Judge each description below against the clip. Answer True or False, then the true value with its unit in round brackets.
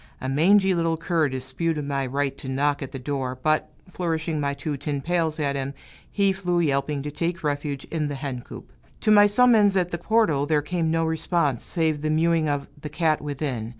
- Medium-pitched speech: True (155 Hz)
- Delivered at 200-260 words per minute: True (205 wpm)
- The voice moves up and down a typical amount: True (3.2 semitones)